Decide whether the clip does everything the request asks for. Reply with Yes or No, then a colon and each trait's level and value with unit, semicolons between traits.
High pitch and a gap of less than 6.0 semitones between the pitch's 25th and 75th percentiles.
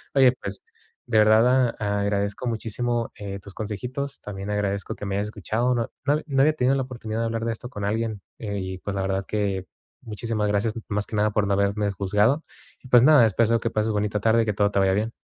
No: low, 105 Hz; narrow, 2.5 semitones